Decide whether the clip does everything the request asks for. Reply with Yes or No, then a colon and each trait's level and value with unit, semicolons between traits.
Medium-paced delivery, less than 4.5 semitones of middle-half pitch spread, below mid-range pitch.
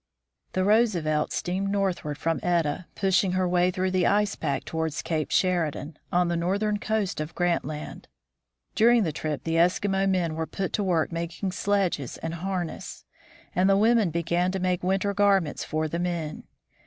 No: average, 175 wpm; average, 3.1 semitones; medium, 180 Hz